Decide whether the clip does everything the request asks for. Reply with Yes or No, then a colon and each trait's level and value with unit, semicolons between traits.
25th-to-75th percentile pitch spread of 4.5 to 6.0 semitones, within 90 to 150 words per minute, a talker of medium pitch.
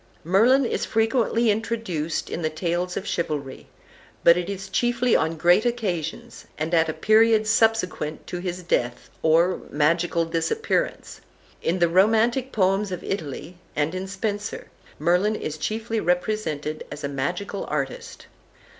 Yes: average, 5.1 semitones; average, 140 wpm; medium, 180 Hz